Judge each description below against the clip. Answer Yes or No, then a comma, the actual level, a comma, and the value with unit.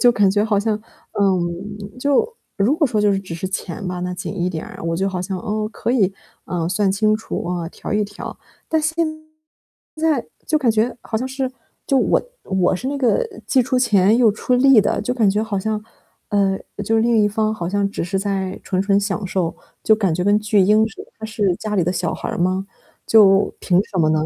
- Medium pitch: No, high, 205 Hz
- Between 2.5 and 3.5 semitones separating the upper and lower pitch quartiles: Yes, average, 2.9 semitones